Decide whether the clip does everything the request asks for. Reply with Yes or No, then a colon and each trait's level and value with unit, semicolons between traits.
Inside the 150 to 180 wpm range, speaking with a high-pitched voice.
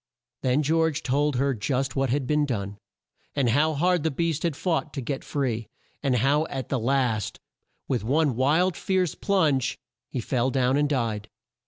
No: average, 175 wpm; low, 135 Hz